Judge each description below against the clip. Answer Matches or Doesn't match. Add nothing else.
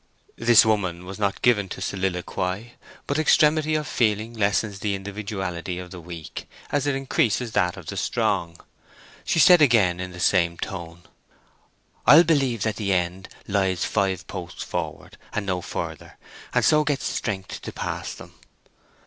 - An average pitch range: Matches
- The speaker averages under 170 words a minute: Matches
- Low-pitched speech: Matches